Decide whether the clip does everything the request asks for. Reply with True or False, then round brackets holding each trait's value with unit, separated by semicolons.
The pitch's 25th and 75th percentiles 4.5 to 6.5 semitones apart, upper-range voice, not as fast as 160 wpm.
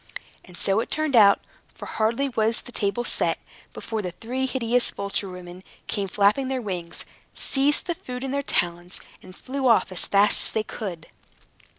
False (5.0 semitones; 220 Hz; 180 wpm)